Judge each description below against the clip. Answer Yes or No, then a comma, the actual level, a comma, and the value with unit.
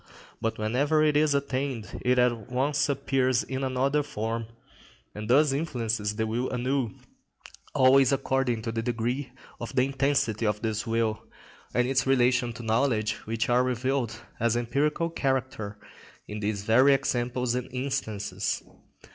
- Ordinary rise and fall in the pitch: Yes, average, 3.2 semitones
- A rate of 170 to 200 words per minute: No, average, 145 wpm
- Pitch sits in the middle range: No, low, 125 Hz